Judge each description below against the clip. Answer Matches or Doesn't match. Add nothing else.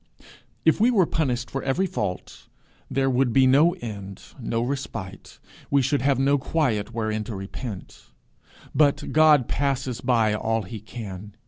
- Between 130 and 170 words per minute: Matches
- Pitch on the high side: Doesn't match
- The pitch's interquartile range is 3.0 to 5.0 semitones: Matches